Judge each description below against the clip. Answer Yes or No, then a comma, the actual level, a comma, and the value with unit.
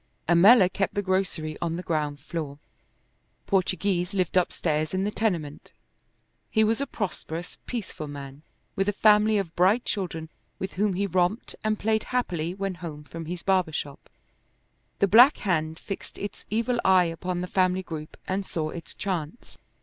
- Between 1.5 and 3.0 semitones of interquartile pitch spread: No, average, 3.8 semitones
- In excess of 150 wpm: Yes, average, 165 wpm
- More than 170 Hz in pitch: Yes, medium, 185 Hz